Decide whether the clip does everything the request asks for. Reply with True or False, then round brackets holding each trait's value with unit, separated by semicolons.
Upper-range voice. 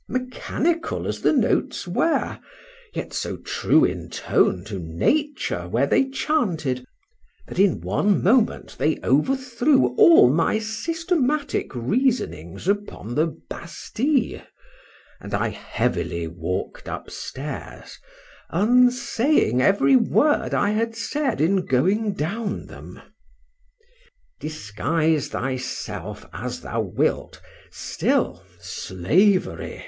True (195 Hz)